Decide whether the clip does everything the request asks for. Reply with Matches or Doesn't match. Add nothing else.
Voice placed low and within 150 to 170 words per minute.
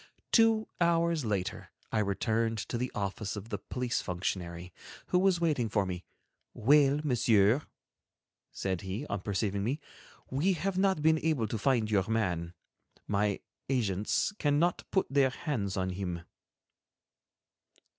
Doesn't match